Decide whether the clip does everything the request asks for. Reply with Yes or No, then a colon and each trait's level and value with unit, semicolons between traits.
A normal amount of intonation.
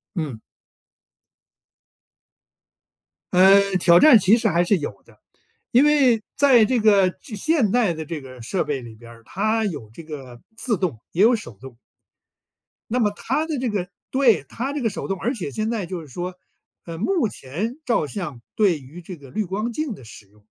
No: wide, 7.4 semitones